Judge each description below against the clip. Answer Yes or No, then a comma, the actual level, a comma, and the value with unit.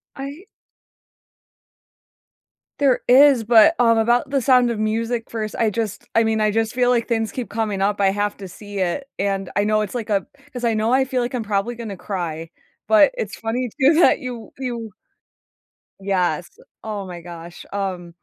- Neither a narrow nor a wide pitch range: Yes, average, 3.5 semitones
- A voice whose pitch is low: No, high, 220 Hz